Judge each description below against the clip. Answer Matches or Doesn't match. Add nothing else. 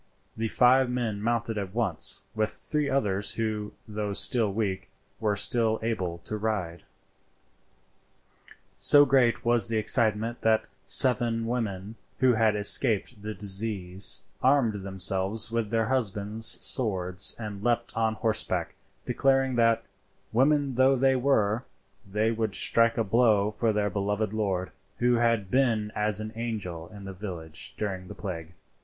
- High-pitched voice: Doesn't match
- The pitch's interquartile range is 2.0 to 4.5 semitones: Matches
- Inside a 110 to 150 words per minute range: Matches